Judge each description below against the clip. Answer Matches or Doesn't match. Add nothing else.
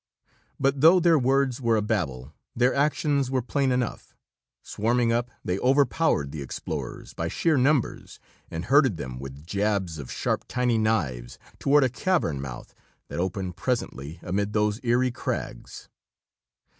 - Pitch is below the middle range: Matches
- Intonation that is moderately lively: Doesn't match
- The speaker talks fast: Doesn't match